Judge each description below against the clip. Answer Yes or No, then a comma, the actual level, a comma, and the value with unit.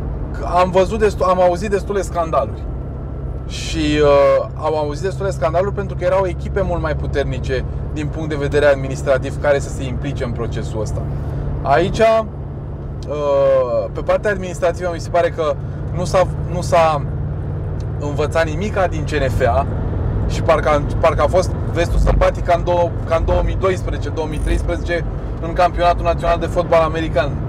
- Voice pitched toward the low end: No, medium, 145 Hz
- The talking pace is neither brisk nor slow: Yes, average, 145 wpm